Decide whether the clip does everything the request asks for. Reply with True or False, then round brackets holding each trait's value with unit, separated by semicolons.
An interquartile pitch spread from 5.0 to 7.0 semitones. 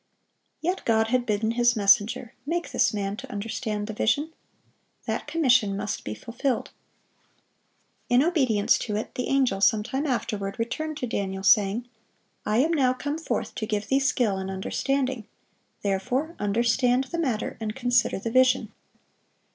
False (4.3 semitones)